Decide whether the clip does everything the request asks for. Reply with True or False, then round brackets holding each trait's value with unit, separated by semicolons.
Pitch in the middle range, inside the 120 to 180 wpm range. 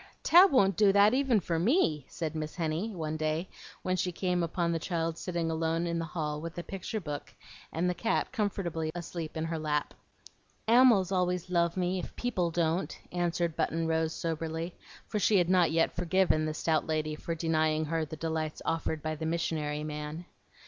False (165 Hz; 190 wpm)